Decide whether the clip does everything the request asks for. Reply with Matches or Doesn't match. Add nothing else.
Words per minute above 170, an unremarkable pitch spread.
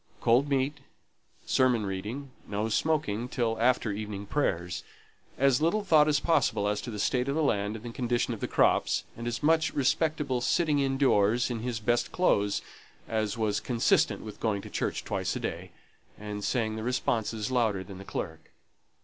Matches